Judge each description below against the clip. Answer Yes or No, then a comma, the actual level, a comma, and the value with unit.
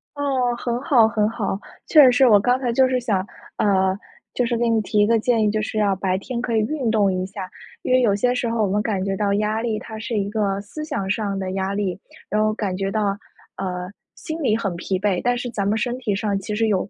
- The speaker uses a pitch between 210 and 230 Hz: Yes, high, 215 Hz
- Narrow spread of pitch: No, average, 3.3 semitones